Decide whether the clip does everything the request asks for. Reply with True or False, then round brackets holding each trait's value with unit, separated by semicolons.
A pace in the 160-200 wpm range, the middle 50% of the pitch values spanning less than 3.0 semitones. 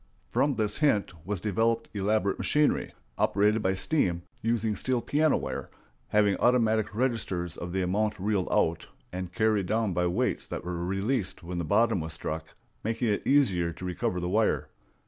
False (165 wpm; 3.9 semitones)